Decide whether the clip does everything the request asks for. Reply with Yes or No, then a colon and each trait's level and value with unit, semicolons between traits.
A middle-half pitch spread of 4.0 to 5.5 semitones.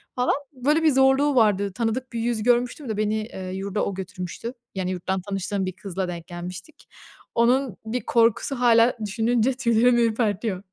Yes: average, 4.3 semitones